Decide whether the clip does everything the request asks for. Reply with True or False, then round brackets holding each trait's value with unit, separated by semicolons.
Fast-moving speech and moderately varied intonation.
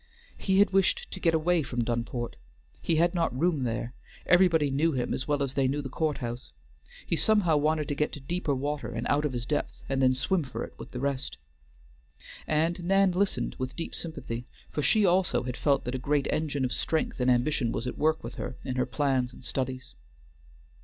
True (210 wpm; 4.3 semitones)